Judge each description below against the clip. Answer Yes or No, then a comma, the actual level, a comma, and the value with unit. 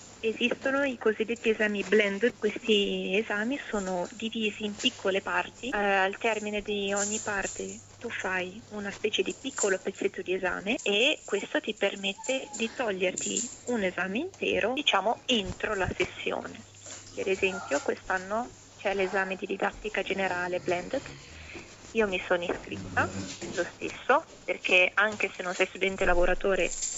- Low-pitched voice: No, high, 210 Hz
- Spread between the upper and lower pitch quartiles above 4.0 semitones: No, average, 3.5 semitones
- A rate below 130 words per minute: No, average, 135 wpm